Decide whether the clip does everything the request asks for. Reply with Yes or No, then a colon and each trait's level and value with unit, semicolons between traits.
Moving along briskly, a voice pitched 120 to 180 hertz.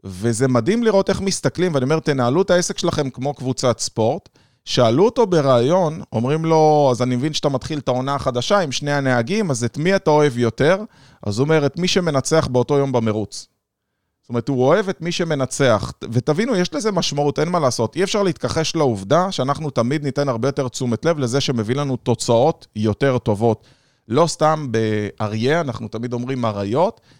Yes: fast, 185 wpm; low, 135 Hz